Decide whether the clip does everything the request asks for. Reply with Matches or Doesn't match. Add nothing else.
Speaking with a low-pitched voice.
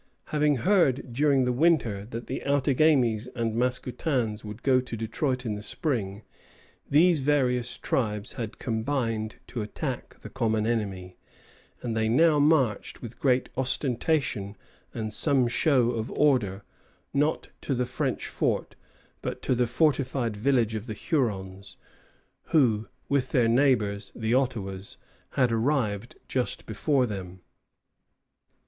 Matches